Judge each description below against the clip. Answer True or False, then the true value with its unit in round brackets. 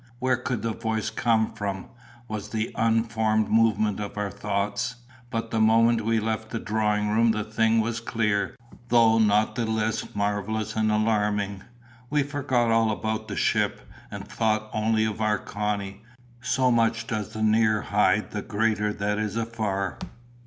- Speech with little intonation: True (1.4 semitones)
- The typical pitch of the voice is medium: False (110 Hz)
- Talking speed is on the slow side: False (160 wpm)